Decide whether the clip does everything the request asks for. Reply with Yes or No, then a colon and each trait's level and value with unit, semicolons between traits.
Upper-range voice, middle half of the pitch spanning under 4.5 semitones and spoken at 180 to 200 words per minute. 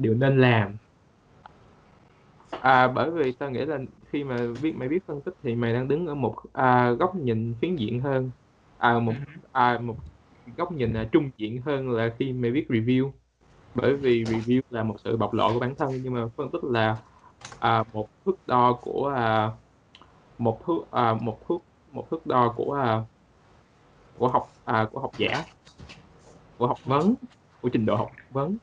No: low, 120 Hz; average, 3.5 semitones; average, 185 wpm